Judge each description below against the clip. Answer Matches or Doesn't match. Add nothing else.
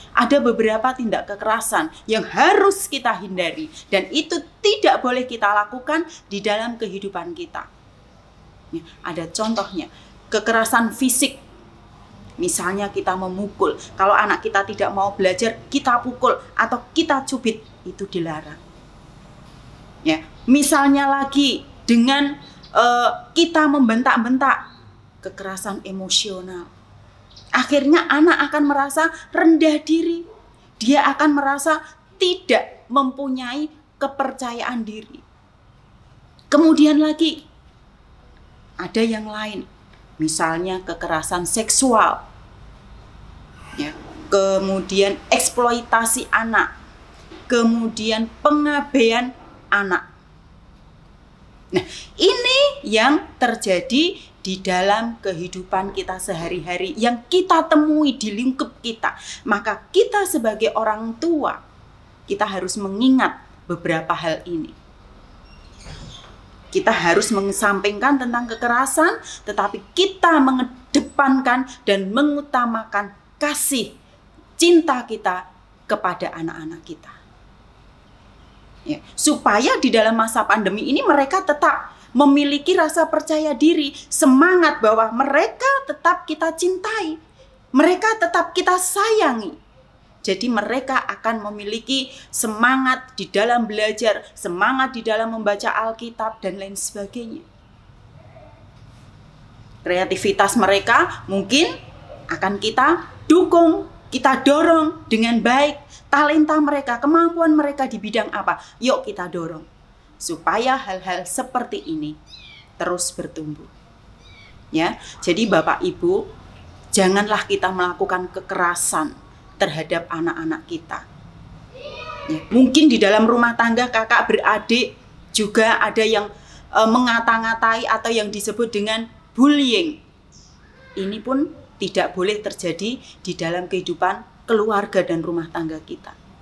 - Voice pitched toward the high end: Matches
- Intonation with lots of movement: Matches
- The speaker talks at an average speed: Matches